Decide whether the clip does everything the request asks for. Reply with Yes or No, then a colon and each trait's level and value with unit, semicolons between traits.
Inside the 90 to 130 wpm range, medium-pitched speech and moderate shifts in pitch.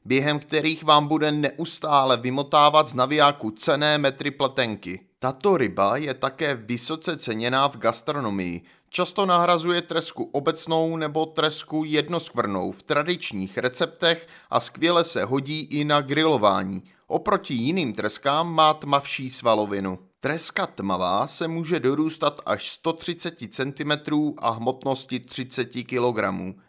Yes: average, 120 wpm; medium, 145 Hz; average, 4.3 semitones